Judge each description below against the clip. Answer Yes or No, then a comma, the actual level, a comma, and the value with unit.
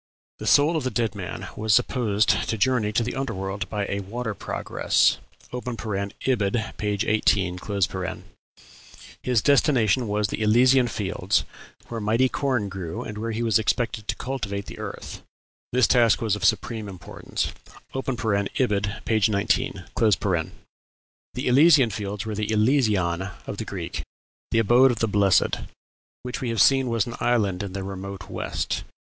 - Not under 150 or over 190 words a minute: Yes, average, 155 wpm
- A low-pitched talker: Yes, low, 110 Hz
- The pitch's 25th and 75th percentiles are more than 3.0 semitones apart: Yes, average, 3.5 semitones